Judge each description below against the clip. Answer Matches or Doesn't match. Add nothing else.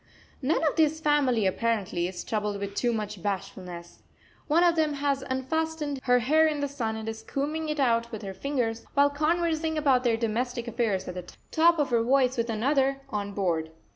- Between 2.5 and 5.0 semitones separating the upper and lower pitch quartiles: Doesn't match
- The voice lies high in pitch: Matches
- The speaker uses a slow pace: Doesn't match